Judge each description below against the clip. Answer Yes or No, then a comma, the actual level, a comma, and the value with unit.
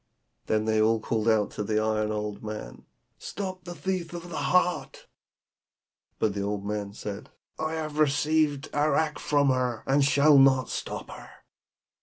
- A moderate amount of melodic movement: No, wide, 6.3 semitones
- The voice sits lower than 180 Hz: Yes, low, 135 Hz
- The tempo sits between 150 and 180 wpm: Yes, average, 155 wpm